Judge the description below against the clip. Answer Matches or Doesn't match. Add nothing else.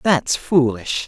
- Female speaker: Doesn't match